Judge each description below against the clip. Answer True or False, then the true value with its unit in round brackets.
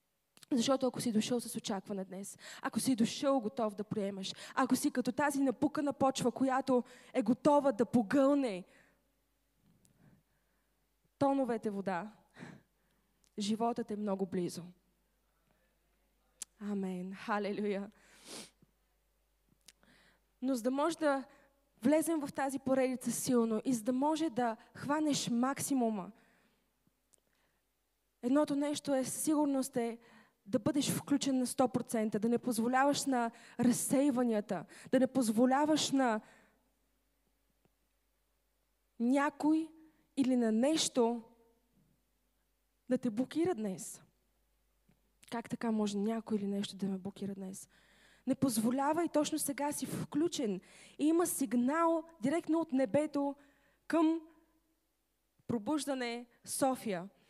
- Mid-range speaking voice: False (250 Hz)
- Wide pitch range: False (4.4 semitones)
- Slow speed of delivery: True (105 wpm)